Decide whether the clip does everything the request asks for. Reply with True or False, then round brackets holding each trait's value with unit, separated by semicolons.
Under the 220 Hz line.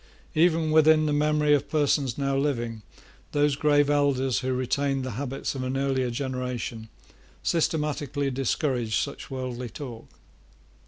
True (140 Hz)